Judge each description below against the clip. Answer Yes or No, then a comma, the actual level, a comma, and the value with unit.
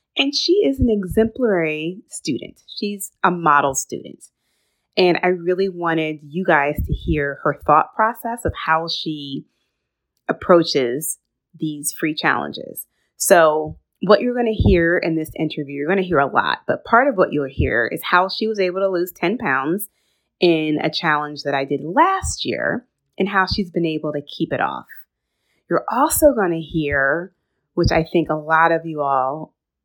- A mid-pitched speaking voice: Yes, medium, 165 Hz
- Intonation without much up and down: No, average, 3.9 semitones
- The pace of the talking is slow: No, average, 170 wpm